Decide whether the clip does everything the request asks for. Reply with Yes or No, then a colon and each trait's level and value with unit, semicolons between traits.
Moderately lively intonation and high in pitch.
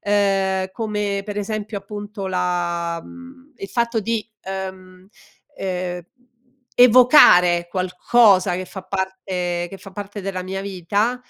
No: narrow, 2.3 semitones; high, 195 Hz